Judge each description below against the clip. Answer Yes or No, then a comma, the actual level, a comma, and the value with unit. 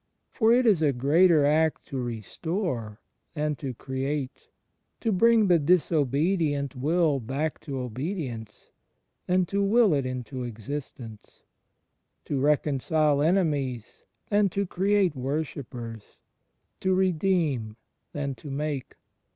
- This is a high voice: No, medium, 150 Hz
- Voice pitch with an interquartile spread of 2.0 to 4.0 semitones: No, wide, 5.5 semitones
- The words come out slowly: Yes, slow, 120 wpm